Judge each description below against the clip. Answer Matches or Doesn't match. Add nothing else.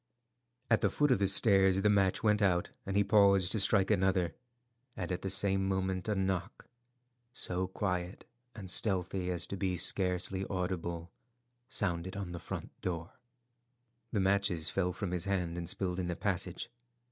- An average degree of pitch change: Doesn't match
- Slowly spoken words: Doesn't match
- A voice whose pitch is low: Matches